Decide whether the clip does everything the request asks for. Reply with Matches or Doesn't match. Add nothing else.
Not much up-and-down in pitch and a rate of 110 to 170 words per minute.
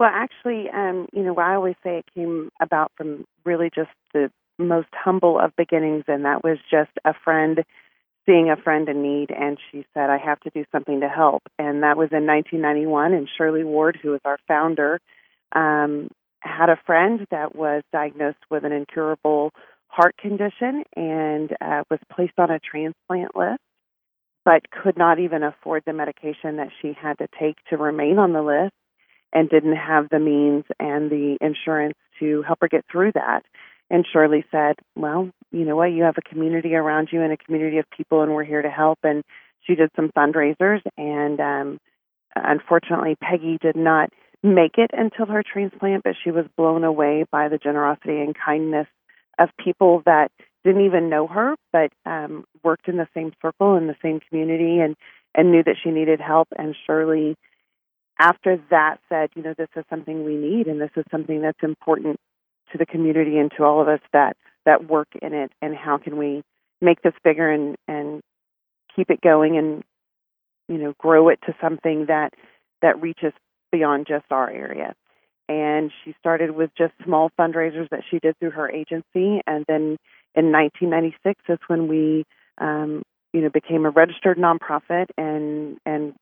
Doesn't match